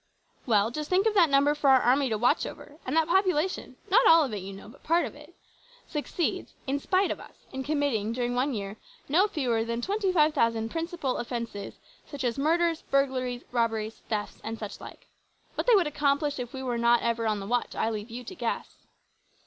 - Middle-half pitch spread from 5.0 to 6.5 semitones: Yes, average, 5.3 semitones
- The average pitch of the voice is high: Yes, very high, 265 Hz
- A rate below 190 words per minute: No, fast, 205 wpm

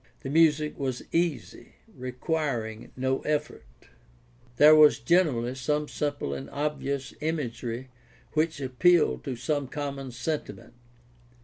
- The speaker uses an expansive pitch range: No, average, 3.1 semitones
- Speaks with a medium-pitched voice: Yes, medium, 145 Hz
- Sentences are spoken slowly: Yes, slow, 110 wpm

